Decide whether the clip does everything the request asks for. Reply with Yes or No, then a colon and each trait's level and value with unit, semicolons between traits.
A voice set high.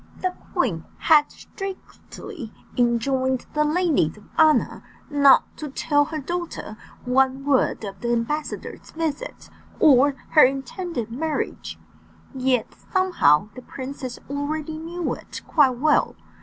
Yes: very high, 280 Hz